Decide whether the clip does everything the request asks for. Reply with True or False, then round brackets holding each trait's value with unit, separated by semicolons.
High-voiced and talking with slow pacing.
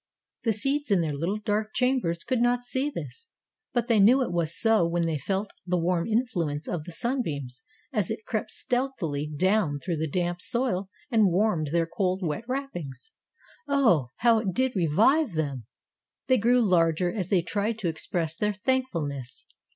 False (195 Hz; 175 wpm)